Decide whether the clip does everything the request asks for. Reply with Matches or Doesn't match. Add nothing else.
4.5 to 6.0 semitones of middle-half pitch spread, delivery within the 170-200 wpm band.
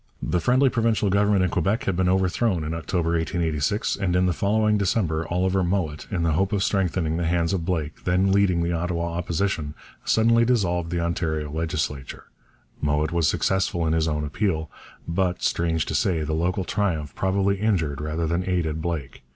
Doesn't match